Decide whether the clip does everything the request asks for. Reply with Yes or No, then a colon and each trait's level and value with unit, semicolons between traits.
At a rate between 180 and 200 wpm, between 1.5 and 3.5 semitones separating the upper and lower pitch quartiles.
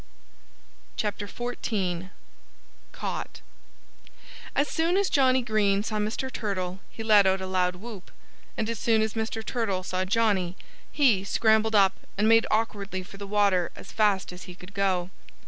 No: average, 150 wpm; average, 3.0 semitones